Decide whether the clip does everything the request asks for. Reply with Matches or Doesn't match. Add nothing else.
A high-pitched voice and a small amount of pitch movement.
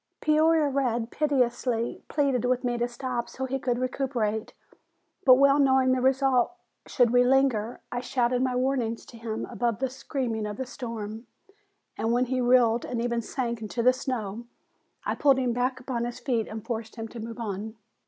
Matches